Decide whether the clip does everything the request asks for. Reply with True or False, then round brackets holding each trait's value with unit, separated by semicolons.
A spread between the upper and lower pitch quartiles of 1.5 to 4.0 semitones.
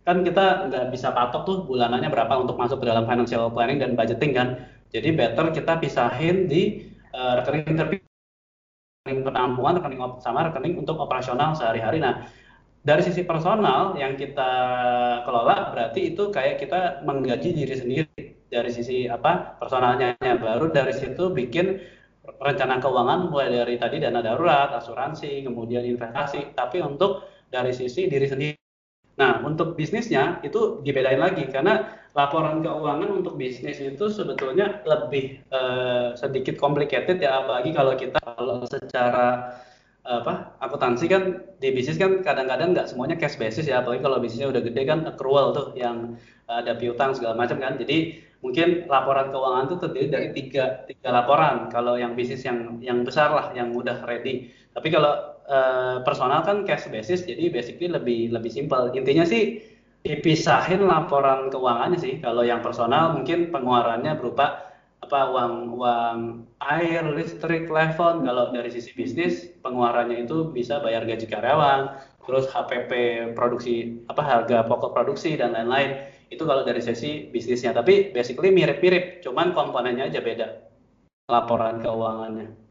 False (5.0 semitones)